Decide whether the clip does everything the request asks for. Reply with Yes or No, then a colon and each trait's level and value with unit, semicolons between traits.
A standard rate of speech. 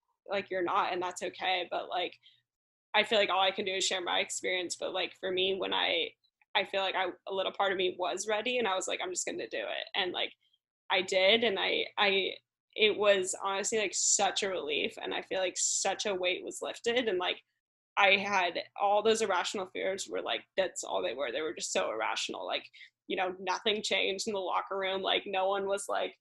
No: fast, 235 wpm